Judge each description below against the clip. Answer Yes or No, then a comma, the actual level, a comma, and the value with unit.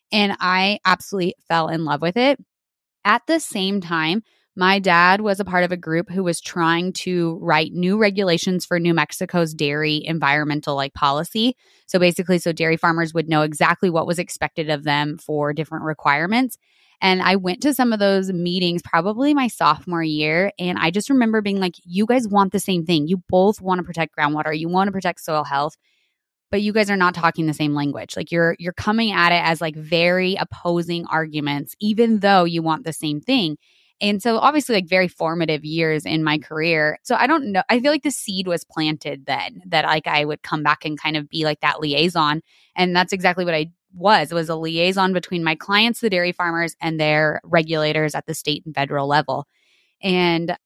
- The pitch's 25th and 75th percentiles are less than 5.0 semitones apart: Yes, average, 3.6 semitones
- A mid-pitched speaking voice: Yes, medium, 170 Hz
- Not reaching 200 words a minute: No, fast, 205 wpm